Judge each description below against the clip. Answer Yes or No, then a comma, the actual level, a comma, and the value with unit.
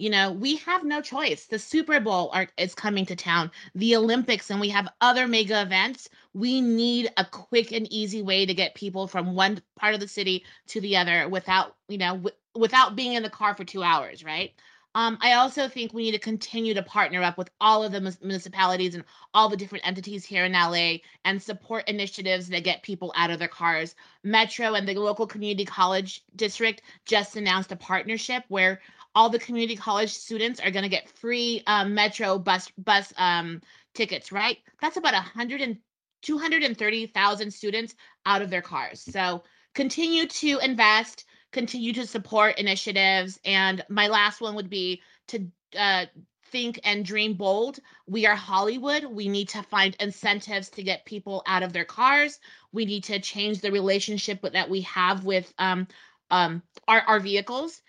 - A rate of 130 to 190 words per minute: Yes, average, 180 wpm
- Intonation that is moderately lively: Yes, average, 3.0 semitones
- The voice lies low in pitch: No, high, 205 Hz